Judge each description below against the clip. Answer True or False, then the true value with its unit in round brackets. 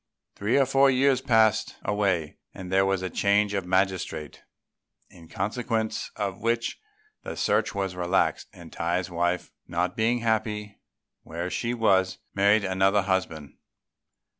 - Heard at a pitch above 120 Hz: False (100 Hz)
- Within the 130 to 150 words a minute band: True (140 wpm)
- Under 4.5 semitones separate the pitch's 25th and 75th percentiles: True (3.4 semitones)